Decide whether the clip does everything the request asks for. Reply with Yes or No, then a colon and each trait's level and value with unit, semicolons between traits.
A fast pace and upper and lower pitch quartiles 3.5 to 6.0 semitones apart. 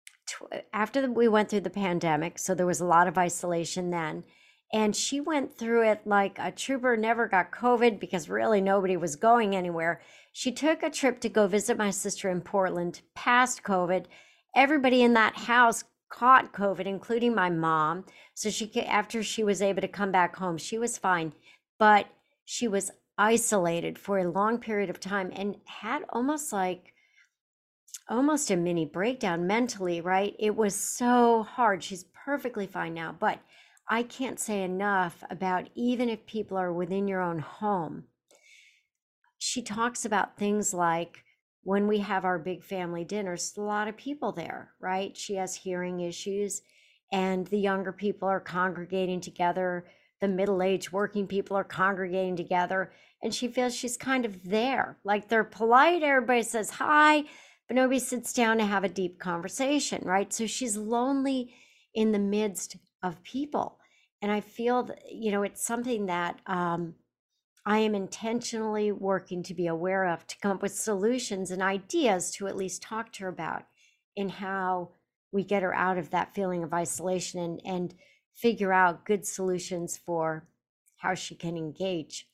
No: average, 170 wpm; average, 3.9 semitones